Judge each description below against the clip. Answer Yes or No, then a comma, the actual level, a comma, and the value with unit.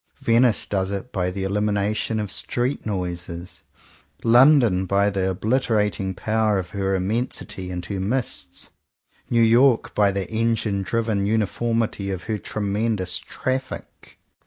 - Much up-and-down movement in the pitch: No, average, 3.1 semitones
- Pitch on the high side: No, low, 105 Hz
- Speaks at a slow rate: Yes, slow, 130 wpm